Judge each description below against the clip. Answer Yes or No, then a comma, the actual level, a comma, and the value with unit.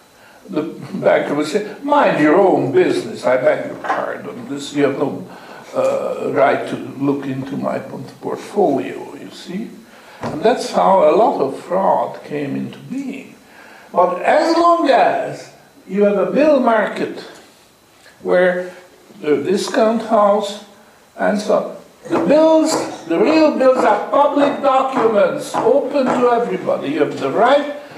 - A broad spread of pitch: Yes, wide, 7.9 semitones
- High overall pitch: Yes, high, 225 Hz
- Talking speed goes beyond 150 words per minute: No, average, 145 wpm